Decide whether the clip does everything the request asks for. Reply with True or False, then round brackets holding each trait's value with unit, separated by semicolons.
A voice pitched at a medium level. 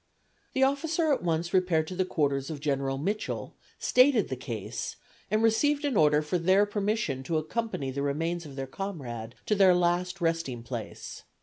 True (170 Hz)